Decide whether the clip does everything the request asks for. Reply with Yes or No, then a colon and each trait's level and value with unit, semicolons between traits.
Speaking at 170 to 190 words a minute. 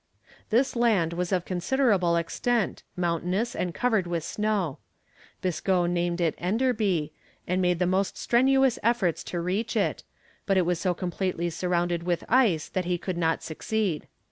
No: average, 155 wpm